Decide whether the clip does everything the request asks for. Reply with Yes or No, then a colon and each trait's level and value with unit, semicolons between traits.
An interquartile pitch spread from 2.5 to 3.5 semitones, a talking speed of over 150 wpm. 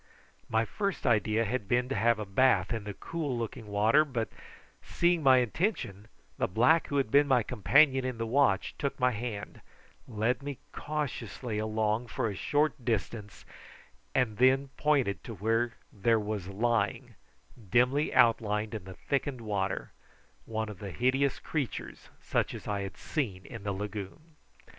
No: average, 4.2 semitones; average, 160 wpm